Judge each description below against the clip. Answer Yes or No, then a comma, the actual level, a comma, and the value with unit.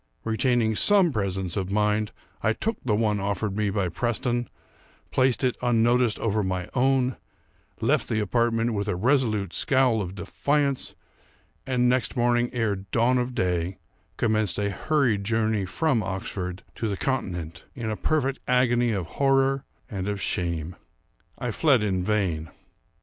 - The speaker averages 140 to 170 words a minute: Yes, average, 150 wpm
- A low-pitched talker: Yes, low, 110 Hz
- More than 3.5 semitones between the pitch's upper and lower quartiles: Yes, average, 4.2 semitones